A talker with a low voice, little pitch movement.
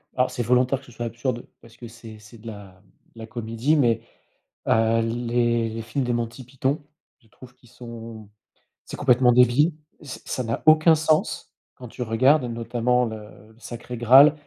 Yes: low, 120 Hz; narrow, 2.1 semitones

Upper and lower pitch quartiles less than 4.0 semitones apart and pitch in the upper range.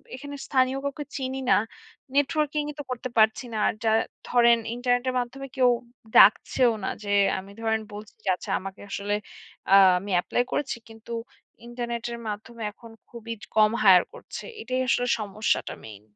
Yes: average, 3.2 semitones; high, 235 Hz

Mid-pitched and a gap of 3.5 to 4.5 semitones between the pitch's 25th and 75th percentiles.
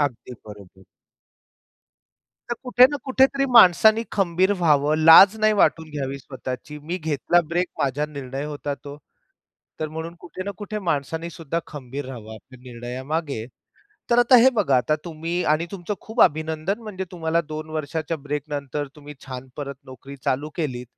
Yes: medium, 155 Hz; average, 4.1 semitones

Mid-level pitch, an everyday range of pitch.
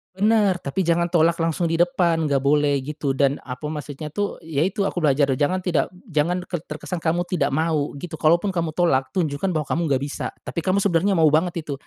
Yes: medium, 165 Hz; average, 3.3 semitones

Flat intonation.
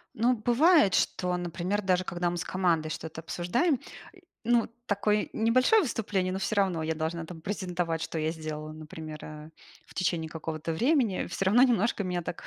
No: average, 4.6 semitones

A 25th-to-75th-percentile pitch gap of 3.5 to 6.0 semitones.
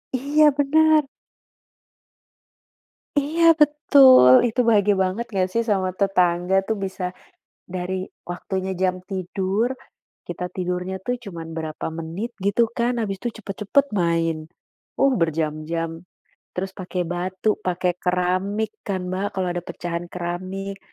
Yes: average, 3.8 semitones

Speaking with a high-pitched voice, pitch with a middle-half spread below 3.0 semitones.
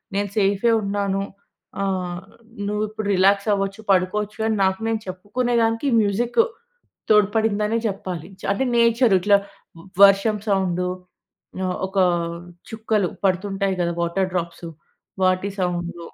Yes: high, 200 Hz; narrow, 2.5 semitones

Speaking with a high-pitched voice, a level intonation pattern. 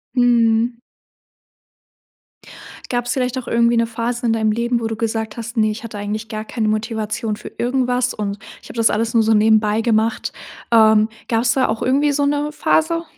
Yes: high, 230 Hz; narrow, 2.0 semitones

